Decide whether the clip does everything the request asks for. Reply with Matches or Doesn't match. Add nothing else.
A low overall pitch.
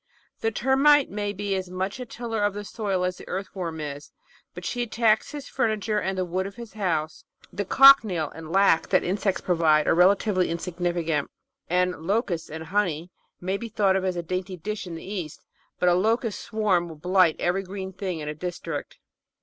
Doesn't match